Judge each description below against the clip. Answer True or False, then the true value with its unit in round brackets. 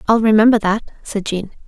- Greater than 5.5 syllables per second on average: True (5.9 syllables/s)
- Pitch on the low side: False (215 Hz)